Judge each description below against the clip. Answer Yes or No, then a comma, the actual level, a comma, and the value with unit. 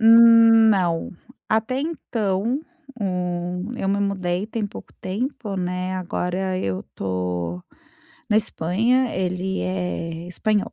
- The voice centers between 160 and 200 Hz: Yes, high, 190 Hz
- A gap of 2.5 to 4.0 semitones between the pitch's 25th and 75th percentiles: Yes, average, 3.7 semitones